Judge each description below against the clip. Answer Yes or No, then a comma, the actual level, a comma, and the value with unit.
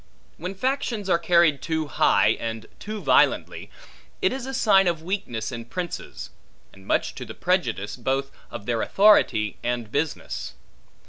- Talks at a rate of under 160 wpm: Yes, average, 150 wpm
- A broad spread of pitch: Yes, wide, 8.9 semitones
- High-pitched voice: No, medium, 160 Hz